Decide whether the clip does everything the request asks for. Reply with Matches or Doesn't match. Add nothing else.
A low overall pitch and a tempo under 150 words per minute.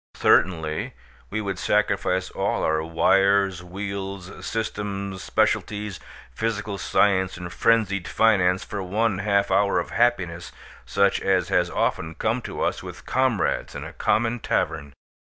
Matches